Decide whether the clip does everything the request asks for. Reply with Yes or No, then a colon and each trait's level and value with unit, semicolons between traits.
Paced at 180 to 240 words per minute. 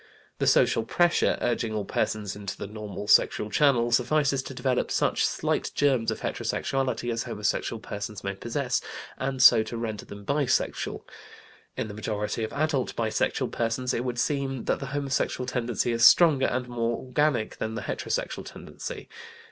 No: average, 165 wpm